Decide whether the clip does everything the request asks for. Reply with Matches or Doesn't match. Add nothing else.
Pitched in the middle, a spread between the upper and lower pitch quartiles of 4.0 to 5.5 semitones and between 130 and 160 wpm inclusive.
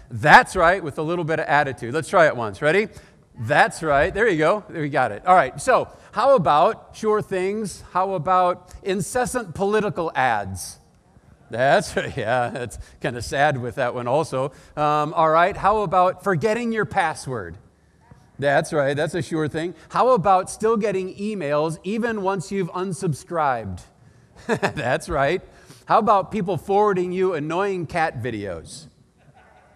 Matches